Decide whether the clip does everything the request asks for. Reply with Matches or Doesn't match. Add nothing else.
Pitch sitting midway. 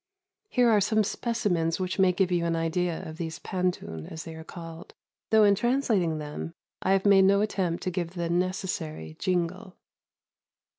Matches